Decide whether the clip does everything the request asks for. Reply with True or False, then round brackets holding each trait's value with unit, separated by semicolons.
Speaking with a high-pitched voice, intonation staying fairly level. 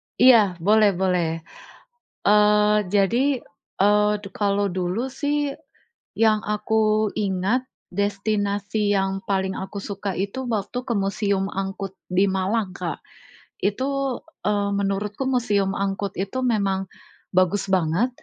True (205 Hz; 2.0 semitones)